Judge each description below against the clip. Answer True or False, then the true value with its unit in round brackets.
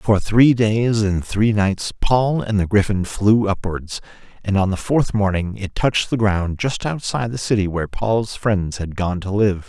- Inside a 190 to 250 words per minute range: True (200 wpm)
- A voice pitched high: False (105 Hz)